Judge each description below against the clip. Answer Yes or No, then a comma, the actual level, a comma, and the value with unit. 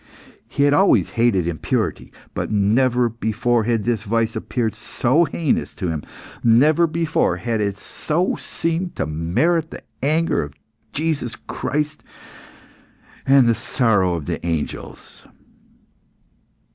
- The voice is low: Yes, low, 120 Hz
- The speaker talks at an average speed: No, slow, 125 wpm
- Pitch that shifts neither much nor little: No, wide, 6.7 semitones